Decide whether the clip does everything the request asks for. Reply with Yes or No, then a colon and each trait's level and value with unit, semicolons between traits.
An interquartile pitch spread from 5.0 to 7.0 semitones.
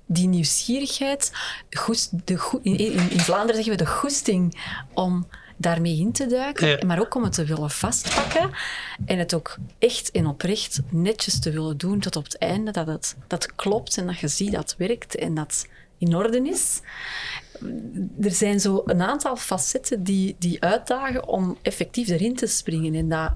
Yes: average, 5.3 semitones